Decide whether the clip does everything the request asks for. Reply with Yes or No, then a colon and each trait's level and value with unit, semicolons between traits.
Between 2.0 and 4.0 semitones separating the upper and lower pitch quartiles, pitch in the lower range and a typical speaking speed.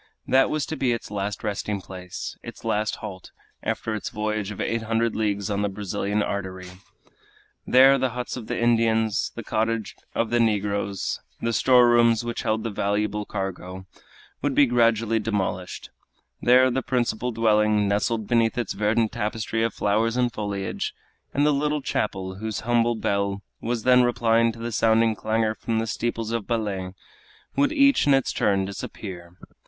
Yes: narrow, 2.6 semitones; low, 110 Hz; average, 170 wpm